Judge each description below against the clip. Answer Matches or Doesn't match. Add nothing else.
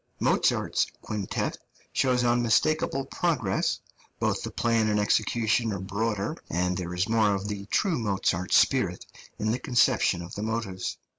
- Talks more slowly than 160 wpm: Matches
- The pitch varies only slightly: Doesn't match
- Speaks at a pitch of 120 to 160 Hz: Doesn't match